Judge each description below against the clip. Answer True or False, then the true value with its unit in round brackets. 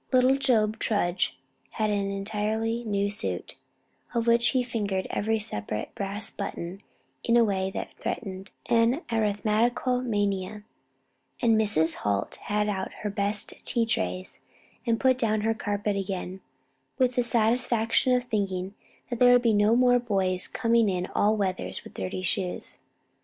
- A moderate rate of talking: True (150 wpm)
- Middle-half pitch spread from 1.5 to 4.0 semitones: True (3.0 semitones)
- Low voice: False (215 Hz)